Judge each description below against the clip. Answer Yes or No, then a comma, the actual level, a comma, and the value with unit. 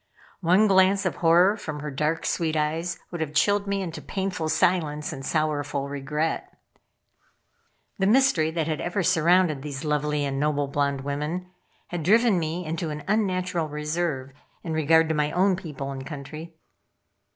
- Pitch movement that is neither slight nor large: Yes, average, 3.4 semitones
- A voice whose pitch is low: No, medium, 160 Hz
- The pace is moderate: Yes, average, 160 wpm